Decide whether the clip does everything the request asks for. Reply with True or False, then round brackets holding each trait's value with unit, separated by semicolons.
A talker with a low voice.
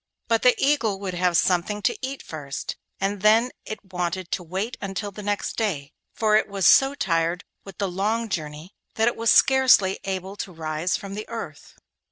False (195 Hz)